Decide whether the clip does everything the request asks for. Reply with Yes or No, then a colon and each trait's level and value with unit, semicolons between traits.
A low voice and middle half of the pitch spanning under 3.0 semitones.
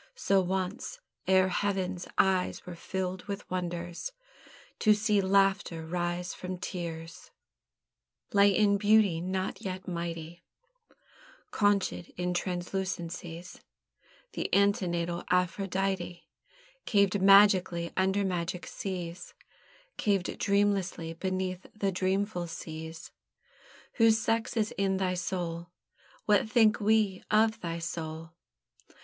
No: medium, 185 Hz; narrow, 2.5 semitones